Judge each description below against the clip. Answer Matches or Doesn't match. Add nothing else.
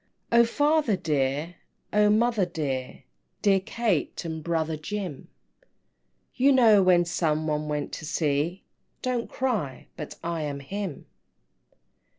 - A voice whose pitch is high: Doesn't match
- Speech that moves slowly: Matches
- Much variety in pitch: Matches